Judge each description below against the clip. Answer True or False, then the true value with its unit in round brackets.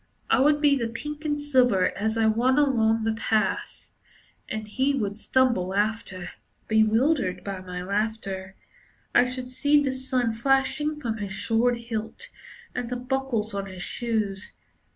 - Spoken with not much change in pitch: False (3.9 semitones)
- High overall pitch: True (230 Hz)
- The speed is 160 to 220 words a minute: False (150 wpm)